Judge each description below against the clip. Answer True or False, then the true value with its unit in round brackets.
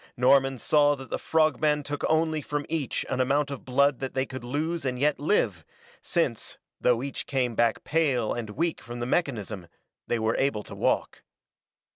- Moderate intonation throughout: True (3.5 semitones)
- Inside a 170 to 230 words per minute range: True (185 wpm)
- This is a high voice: False (135 Hz)